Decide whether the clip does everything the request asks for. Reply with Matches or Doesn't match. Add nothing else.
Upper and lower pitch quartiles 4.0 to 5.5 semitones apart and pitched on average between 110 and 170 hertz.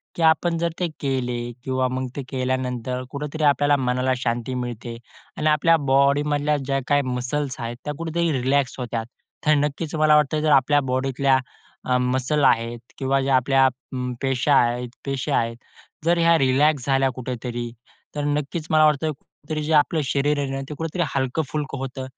Doesn't match